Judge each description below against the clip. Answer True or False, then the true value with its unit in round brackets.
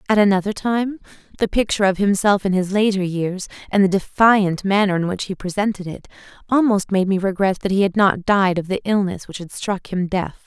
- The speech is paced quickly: True (210 wpm)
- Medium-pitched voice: False (195 Hz)